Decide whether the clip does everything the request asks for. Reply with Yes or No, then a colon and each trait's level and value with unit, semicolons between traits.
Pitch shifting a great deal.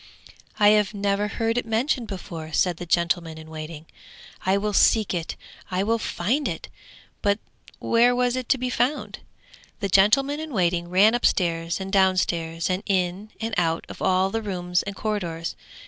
No: average, 4.4 semitones